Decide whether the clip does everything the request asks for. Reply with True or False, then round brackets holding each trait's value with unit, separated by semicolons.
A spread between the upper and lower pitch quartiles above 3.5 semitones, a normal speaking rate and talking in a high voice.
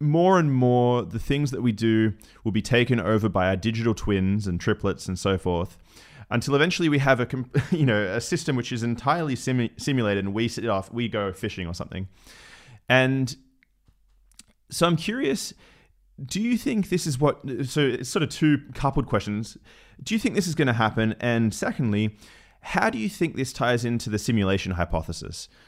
False (5.1 semitones; 190 wpm; 120 Hz)